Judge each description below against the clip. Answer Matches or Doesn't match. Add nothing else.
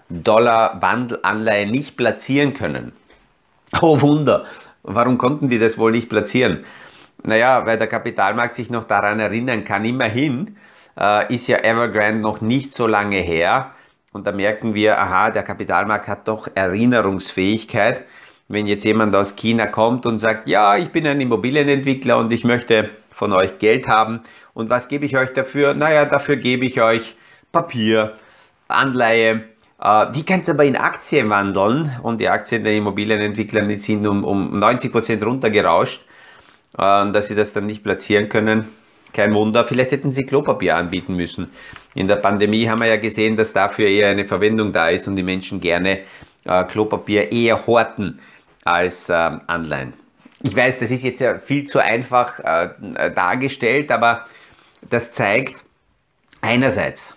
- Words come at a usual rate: Matches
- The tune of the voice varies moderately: Matches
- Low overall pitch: Matches